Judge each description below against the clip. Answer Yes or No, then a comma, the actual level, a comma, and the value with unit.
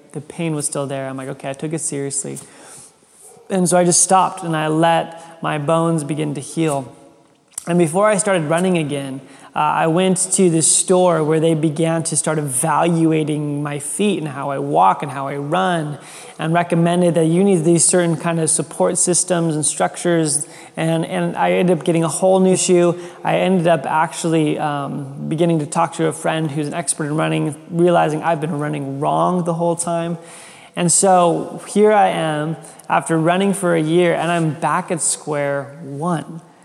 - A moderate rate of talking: Yes, average, 190 wpm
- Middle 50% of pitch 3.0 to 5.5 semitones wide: No, narrow, 2.4 semitones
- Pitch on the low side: No, medium, 165 Hz